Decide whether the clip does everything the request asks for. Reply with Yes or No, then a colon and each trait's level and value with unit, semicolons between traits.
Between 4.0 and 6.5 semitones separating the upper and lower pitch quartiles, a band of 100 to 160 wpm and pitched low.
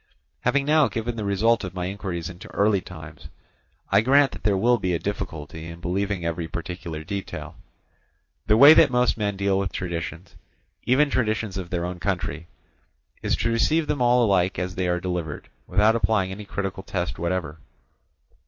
No: average, 4.3 semitones; average, 175 wpm; very low, 95 Hz